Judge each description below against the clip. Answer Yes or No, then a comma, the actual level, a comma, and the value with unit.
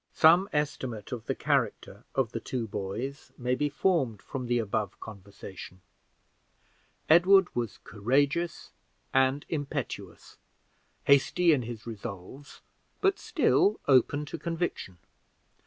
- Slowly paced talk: Yes, slow, 115 wpm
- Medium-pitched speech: No, low, 130 Hz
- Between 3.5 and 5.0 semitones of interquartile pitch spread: No, wide, 5.6 semitones